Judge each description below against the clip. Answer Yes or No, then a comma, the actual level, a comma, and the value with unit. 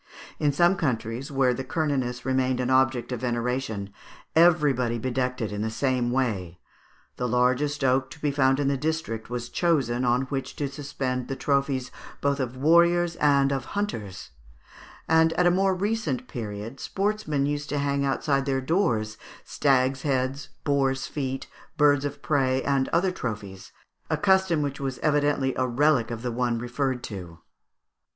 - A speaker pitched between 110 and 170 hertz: Yes, low, 135 Hz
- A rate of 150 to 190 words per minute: Yes, average, 160 wpm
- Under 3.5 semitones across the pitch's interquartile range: Yes, average, 3.0 semitones